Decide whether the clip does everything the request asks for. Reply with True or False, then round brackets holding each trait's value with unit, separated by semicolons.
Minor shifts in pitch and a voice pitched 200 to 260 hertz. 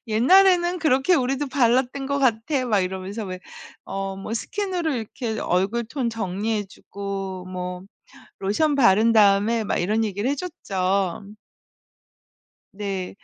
False (5.5 semitones; 220 Hz)